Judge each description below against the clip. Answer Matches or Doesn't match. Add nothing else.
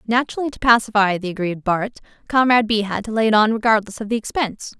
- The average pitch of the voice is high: Matches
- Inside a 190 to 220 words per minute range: Matches